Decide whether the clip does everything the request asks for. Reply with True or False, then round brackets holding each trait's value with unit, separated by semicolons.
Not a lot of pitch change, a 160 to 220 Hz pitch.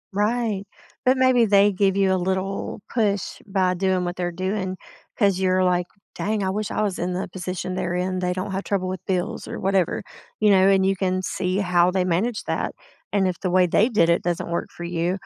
True (1.7 semitones; 190 Hz)